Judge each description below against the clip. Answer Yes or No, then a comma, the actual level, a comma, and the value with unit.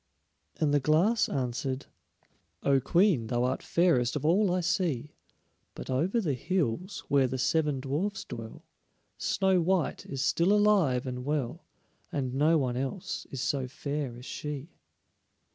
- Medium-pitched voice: Yes, medium, 145 Hz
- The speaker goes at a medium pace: Yes, average, 145 wpm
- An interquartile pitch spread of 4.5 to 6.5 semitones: Yes, wide, 5.5 semitones